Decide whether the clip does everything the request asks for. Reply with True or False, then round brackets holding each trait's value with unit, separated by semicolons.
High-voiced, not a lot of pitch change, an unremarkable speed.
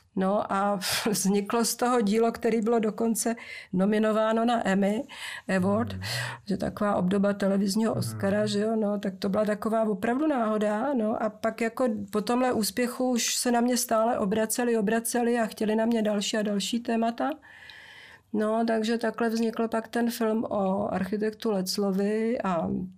True (220 Hz; 2.1 semitones; 155 wpm)